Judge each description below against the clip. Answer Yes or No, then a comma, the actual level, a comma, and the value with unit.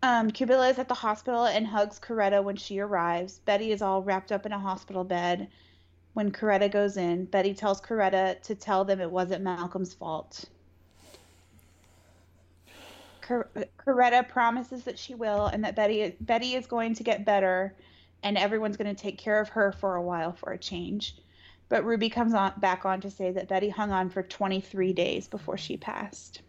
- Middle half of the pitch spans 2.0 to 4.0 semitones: Yes, average, 3.3 semitones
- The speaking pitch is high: Yes, high, 195 Hz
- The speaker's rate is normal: Yes, average, 185 wpm